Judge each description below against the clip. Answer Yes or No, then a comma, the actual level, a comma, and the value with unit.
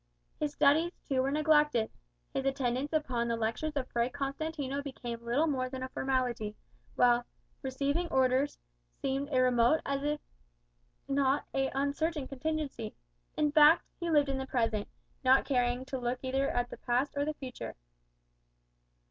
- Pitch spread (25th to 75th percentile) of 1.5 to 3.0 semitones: Yes, average, 2.7 semitones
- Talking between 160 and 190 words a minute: No, average, 150 wpm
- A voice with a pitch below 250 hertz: No, very high, 270 Hz